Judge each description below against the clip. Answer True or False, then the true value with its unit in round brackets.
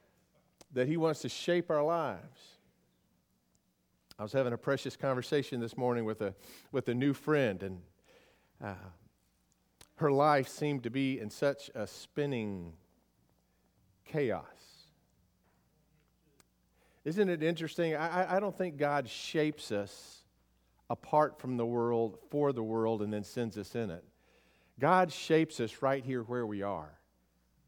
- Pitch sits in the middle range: False (120 Hz)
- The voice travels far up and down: True (7.1 semitones)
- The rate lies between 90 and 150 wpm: True (140 wpm)